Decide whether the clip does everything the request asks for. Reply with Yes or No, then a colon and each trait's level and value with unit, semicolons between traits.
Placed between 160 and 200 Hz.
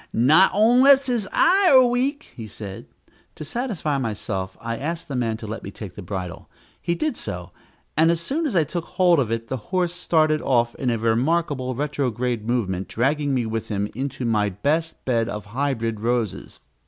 No: low, 130 Hz